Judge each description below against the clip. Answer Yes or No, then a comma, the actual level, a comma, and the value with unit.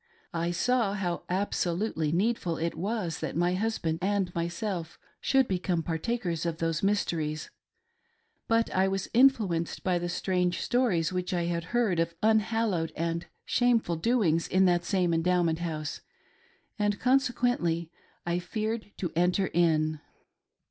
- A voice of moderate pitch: Yes, medium, 180 Hz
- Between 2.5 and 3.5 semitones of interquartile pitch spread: No, average, 4.1 semitones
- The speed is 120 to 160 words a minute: Yes, average, 140 wpm